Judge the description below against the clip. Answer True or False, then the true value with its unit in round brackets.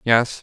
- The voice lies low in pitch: True (115 Hz)